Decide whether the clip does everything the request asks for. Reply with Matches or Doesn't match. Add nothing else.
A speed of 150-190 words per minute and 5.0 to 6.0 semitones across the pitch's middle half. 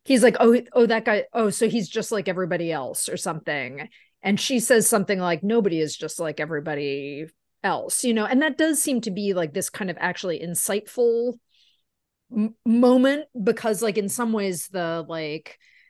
Matches